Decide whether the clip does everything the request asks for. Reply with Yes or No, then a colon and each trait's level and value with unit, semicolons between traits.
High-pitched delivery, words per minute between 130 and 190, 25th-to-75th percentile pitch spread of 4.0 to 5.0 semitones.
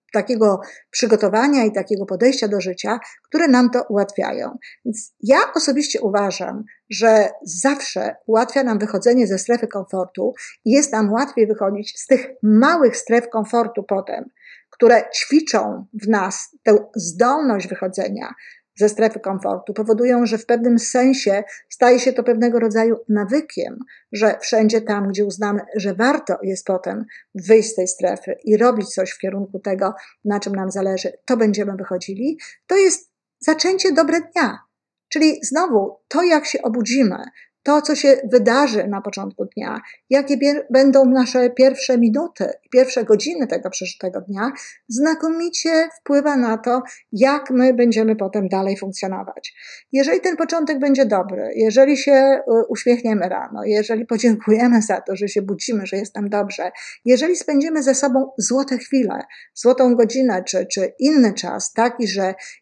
Yes: high, 230 Hz; average, 145 wpm; average, 4.7 semitones